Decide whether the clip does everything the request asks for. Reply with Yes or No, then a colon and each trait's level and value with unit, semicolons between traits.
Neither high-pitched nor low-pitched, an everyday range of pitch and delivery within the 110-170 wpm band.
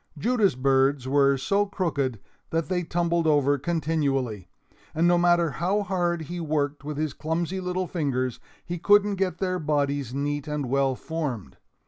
Yes: medium, 155 Hz; average, 4.1 semitones; average, 155 wpm